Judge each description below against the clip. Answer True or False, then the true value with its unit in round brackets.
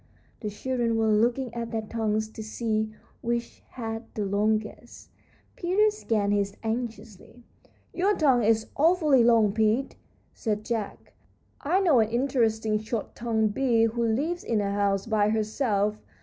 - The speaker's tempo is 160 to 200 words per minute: False (145 wpm)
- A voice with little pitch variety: True (2.3 semitones)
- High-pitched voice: True (225 Hz)